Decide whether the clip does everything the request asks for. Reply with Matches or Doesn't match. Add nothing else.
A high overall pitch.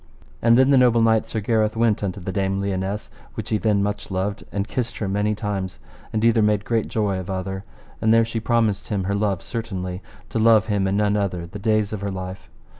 Doesn't match